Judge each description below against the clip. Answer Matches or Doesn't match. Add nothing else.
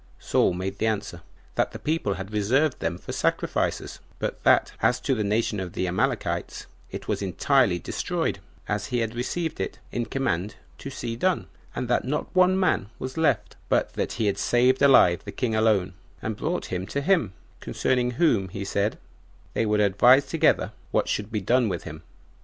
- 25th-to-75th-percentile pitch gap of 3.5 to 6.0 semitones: Matches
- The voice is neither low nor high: Doesn't match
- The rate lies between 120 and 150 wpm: Doesn't match